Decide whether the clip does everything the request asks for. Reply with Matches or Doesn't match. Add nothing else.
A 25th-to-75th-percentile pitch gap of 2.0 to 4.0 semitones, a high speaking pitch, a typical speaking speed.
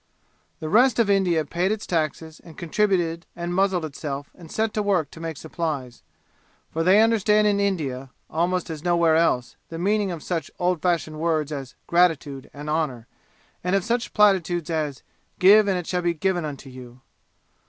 Doesn't match